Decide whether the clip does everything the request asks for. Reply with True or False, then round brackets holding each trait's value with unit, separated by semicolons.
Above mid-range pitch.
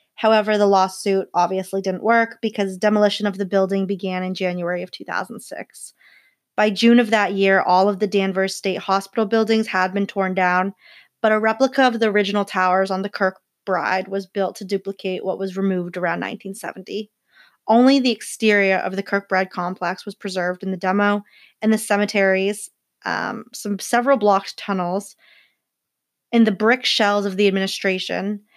True (195 Hz)